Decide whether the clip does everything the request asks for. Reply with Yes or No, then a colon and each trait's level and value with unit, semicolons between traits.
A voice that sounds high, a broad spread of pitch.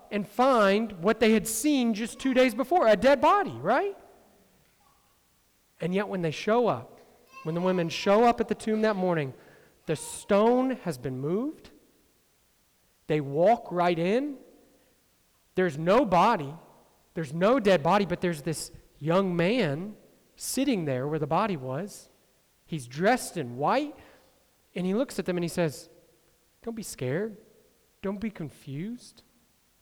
Yes: high, 195 Hz; wide, 5.9 semitones